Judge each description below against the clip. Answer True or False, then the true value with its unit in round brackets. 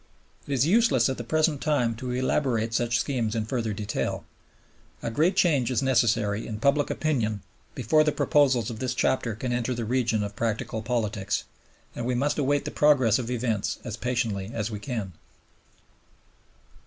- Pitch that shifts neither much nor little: True (3.5 semitones)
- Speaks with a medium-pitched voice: False (120 Hz)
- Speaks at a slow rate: False (170 wpm)